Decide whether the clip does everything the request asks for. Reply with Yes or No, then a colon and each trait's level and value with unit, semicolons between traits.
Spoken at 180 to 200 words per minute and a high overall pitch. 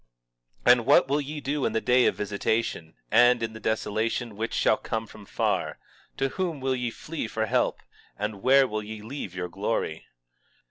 No: average, 190 wpm; low, 115 Hz